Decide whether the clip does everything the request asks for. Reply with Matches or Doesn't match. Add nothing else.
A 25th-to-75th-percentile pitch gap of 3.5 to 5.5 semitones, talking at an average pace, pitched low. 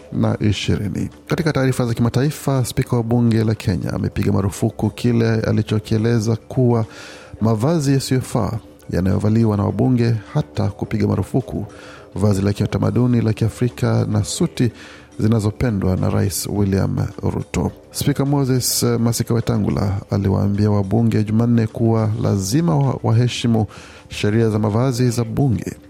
Doesn't match